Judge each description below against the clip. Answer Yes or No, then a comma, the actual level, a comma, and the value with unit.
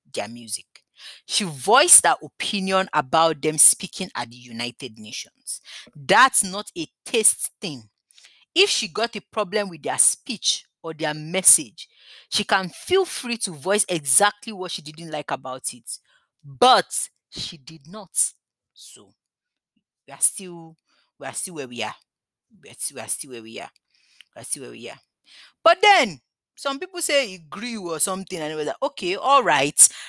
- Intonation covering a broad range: Yes, wide, 6.2 semitones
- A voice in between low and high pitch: Yes, medium, 180 Hz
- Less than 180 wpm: Yes, average, 165 wpm